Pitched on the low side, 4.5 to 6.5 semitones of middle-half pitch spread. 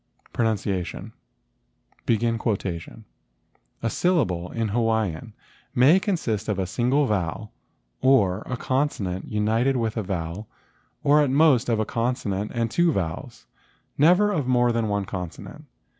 Yes: low, 115 Hz; average, 4.9 semitones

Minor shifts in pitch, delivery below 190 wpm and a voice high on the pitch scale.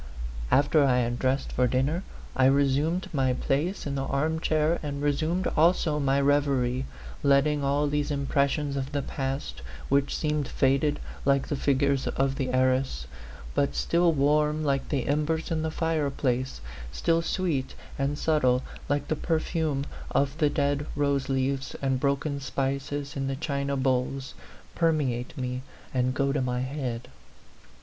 No: narrow, 2.0 semitones; average, 155 wpm; medium, 140 Hz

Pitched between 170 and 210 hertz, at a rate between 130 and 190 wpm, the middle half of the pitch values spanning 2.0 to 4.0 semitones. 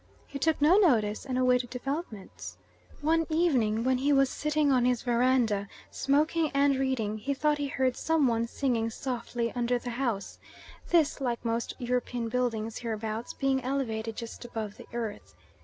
No: very high, 250 Hz; average, 160 wpm; average, 3.3 semitones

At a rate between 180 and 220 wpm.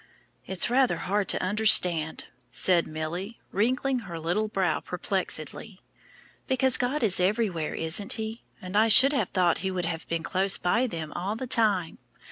No: average, 160 wpm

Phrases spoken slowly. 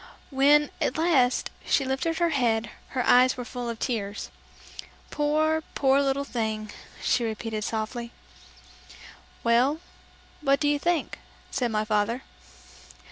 Yes: slow, 130 wpm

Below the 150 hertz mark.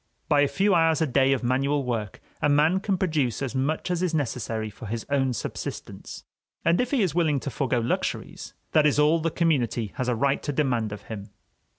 Yes: medium, 140 Hz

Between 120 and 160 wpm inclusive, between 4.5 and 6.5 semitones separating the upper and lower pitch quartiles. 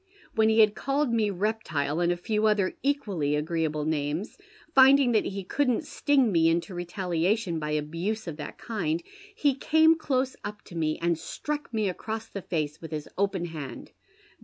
No: average, 175 wpm; wide, 5.6 semitones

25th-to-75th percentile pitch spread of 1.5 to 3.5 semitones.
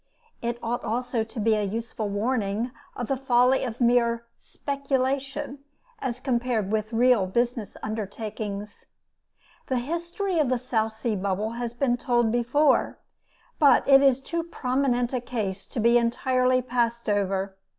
Yes: average, 2.8 semitones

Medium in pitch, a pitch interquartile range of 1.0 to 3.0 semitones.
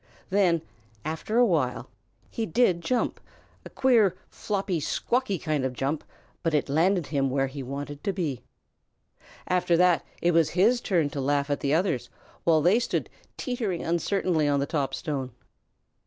No: medium, 165 Hz; average, 5.1 semitones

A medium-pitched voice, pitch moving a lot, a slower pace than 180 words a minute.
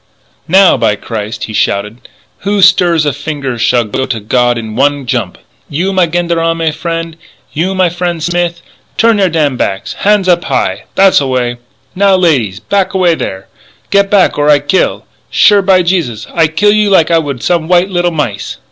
No: medium, 165 Hz; wide, 6.3 semitones; average, 185 wpm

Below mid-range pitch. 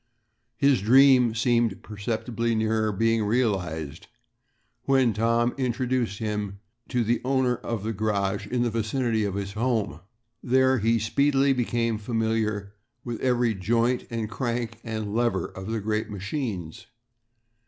Yes: low, 115 Hz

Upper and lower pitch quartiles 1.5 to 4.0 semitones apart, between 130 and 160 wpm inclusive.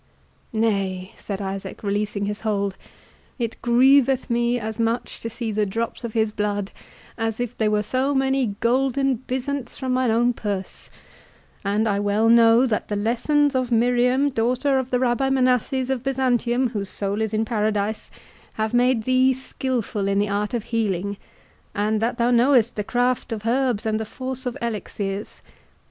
No: average, 3.4 semitones; average, 170 wpm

